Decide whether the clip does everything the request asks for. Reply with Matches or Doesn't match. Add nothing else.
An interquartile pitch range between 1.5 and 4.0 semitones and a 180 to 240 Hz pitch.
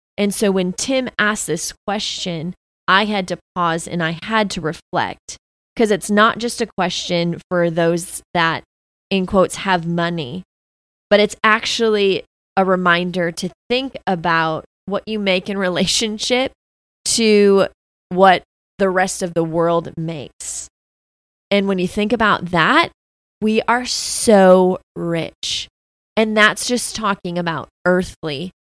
Matches